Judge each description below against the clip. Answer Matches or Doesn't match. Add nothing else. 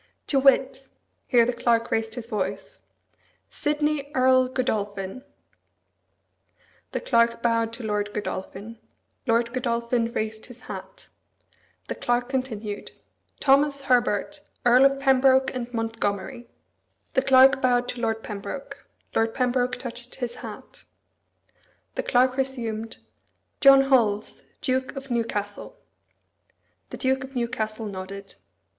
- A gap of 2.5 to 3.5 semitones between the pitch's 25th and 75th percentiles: Matches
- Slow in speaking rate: Matches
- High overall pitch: Matches